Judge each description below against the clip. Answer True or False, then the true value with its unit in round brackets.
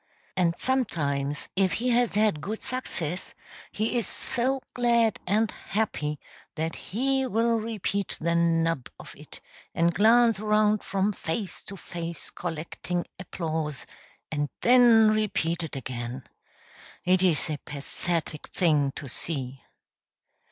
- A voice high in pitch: False (180 Hz)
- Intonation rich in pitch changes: True (5.8 semitones)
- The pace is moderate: False (125 wpm)